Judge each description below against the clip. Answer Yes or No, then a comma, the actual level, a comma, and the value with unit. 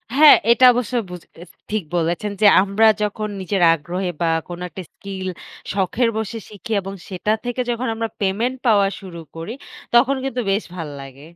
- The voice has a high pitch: Yes, high, 200 Hz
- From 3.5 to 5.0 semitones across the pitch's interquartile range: Yes, average, 4.1 semitones